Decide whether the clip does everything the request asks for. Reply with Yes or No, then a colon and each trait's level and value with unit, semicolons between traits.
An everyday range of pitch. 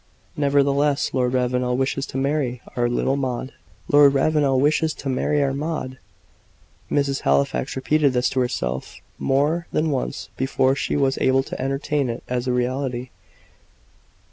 No: narrow, 2.2 semitones